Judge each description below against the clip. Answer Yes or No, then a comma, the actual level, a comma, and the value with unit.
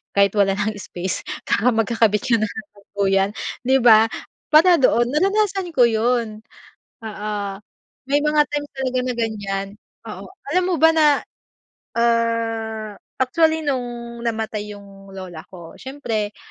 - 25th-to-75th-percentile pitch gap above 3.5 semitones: Yes, average, 4.2 semitones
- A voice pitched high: Yes, high, 225 Hz